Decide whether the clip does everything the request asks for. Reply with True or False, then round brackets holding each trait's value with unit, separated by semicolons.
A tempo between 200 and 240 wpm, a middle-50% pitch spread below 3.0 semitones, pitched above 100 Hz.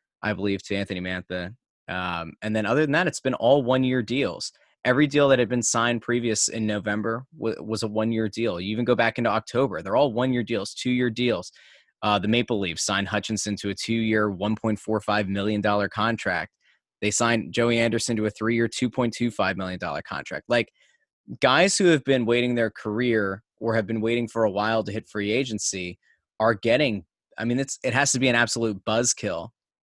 True (205 wpm; 2.6 semitones; 115 Hz)